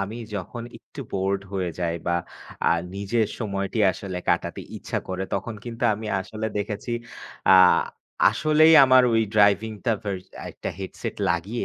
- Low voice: Yes, low, 100 Hz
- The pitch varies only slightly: No, average, 3.2 semitones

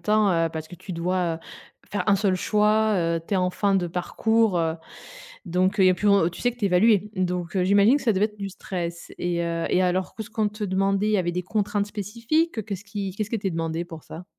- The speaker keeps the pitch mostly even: No, average, 3.0 semitones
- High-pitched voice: Yes, high, 195 Hz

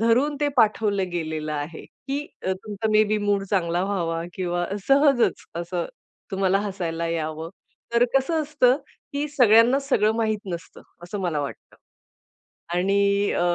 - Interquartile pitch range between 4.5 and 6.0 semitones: Yes, average, 5.2 semitones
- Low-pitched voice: No, high, 200 Hz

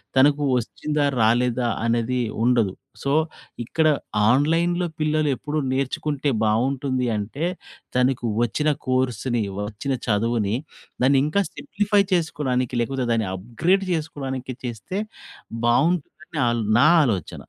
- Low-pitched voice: Yes, low, 130 Hz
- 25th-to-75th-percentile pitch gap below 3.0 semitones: No, average, 4.2 semitones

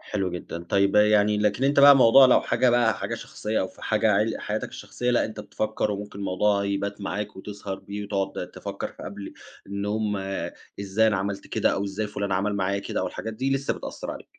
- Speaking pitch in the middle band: No, low, 105 Hz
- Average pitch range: No, narrow, 1.7 semitones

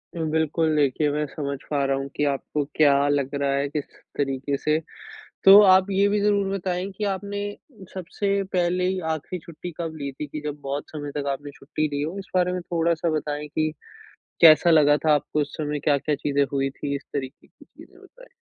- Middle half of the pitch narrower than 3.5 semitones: No, average, 3.8 semitones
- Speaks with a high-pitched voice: No, medium, 150 Hz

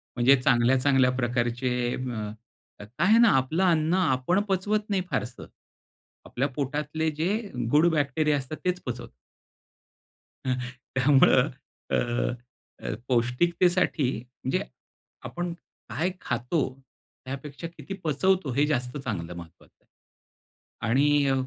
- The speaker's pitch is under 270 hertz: Yes, medium, 140 Hz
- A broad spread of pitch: No, average, 4.9 semitones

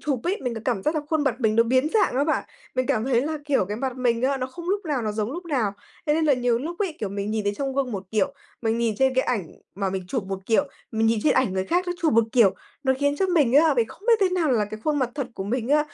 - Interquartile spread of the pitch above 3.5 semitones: Yes, average, 5.1 semitones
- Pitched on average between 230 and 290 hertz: Yes, very high, 255 Hz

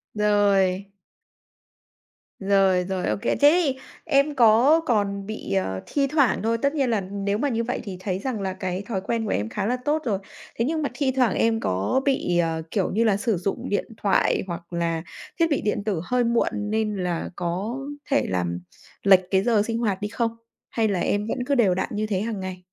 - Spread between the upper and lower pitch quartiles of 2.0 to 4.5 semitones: Yes, average, 4.0 semitones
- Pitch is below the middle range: No, high, 210 Hz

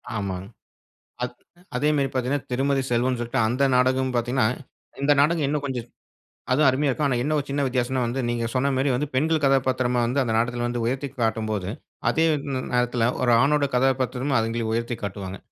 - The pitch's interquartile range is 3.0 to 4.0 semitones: No, narrow, 2.5 semitones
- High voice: No, low, 130 Hz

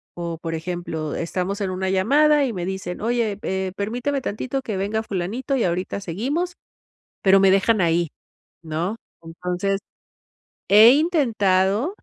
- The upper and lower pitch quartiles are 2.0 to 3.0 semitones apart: No, average, 4.7 semitones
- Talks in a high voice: Yes, high, 195 Hz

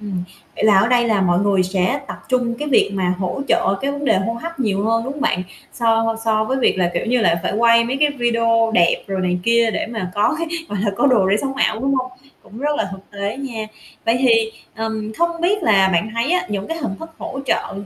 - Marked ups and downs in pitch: No, average, 4.7 semitones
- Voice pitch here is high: Yes, high, 225 Hz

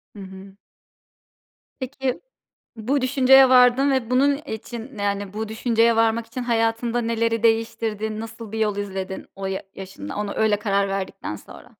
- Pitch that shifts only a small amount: No, average, 3.2 semitones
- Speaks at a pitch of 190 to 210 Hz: No, high, 225 Hz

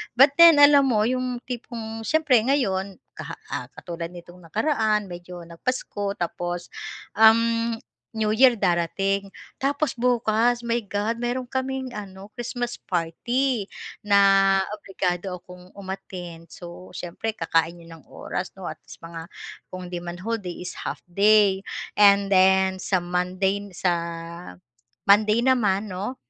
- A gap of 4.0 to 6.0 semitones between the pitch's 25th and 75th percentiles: Yes, average, 4.7 semitones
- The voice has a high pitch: Yes, high, 200 Hz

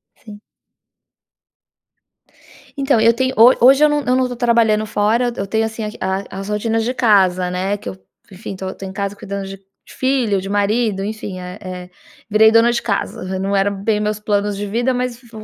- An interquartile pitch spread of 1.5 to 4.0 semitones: Yes, average, 3.1 semitones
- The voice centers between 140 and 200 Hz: No, high, 210 Hz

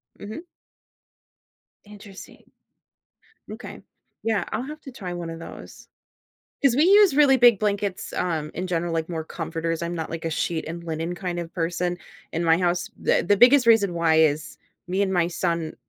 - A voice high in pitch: No, medium, 175 Hz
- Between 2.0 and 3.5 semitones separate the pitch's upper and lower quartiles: No, average, 4.0 semitones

